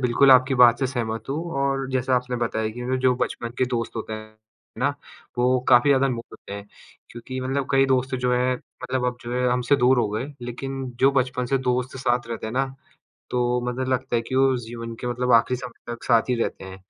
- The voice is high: No, low, 125 Hz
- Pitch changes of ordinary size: No, narrow, 1.6 semitones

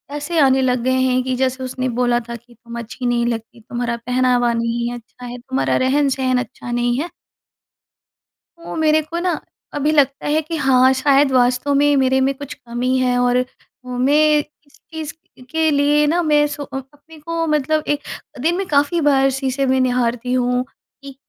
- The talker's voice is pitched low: No, very high, 265 Hz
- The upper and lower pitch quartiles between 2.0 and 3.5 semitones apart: Yes, average, 2.9 semitones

